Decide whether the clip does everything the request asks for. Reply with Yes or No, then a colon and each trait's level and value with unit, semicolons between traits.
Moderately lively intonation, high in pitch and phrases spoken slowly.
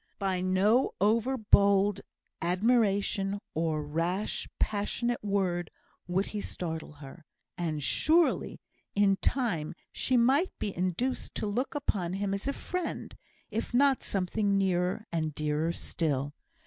Yes: average, 4.3 semitones; high, 195 Hz; slow, 125 wpm